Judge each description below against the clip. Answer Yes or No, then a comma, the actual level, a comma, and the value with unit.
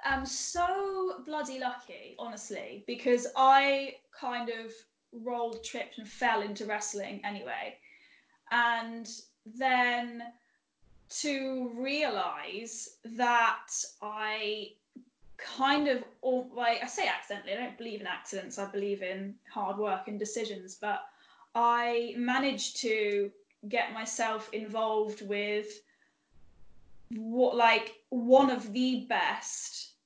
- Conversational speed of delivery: No, slow, 110 wpm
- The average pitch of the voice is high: Yes, high, 235 Hz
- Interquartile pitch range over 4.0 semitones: No, average, 3.0 semitones